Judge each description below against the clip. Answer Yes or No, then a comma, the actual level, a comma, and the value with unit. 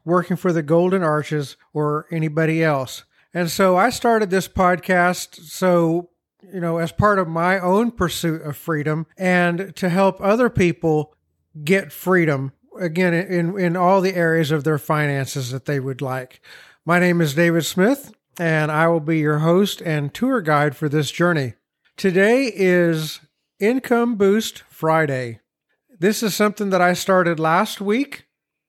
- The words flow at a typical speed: Yes, average, 155 wpm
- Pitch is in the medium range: Yes, medium, 175 Hz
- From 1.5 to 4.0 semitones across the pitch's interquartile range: Yes, average, 3.4 semitones